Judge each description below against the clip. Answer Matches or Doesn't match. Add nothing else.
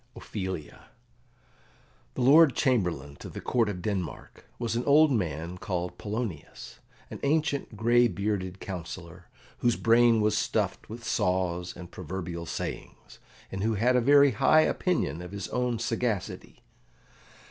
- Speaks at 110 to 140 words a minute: Matches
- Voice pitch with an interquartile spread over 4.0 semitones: Matches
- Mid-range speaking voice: Doesn't match